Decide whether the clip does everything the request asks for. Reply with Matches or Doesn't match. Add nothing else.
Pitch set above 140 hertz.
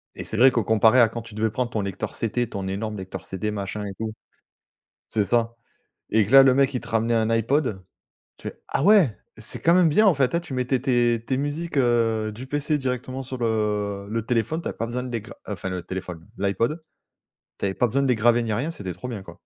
Doesn't match